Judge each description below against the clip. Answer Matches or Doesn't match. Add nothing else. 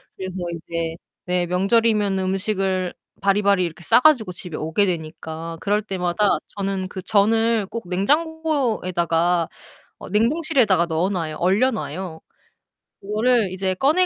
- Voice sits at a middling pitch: Doesn't match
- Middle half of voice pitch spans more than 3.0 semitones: Matches